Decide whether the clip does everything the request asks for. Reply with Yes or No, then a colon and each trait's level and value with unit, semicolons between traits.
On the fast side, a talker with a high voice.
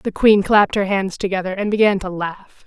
Yes: fast, 225 wpm; high, 195 Hz